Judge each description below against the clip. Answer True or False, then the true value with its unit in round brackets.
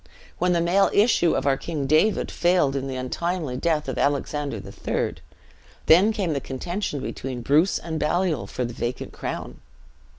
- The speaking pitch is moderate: True (155 Hz)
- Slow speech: False (165 wpm)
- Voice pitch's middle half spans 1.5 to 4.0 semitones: False (4.6 semitones)